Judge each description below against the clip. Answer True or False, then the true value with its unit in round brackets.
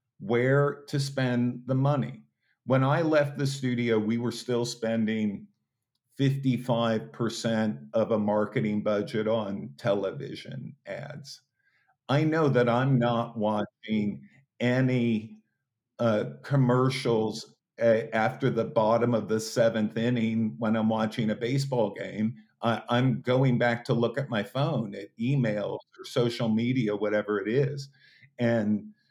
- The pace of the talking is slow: True (130 wpm)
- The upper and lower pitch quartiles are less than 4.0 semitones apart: True (2.9 semitones)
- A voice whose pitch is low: True (120 Hz)